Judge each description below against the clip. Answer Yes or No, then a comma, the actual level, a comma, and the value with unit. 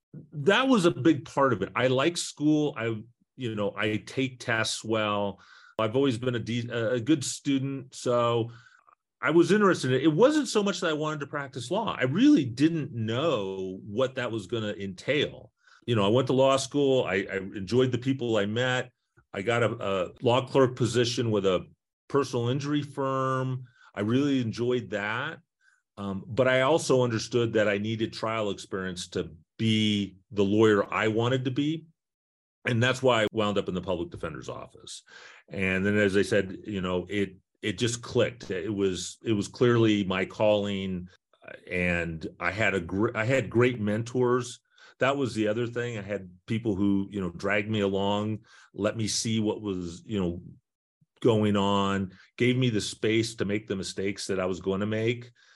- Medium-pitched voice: No, low, 115 Hz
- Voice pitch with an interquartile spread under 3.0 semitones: No, average, 4.3 semitones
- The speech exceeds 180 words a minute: Yes, average, 190 wpm